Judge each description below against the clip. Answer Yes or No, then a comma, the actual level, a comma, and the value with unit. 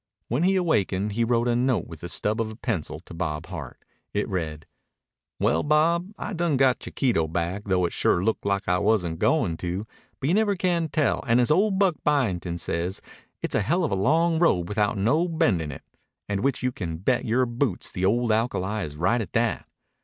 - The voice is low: Yes, low, 110 Hz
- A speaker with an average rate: No, fast, 215 wpm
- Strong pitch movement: Yes, wide, 8.0 semitones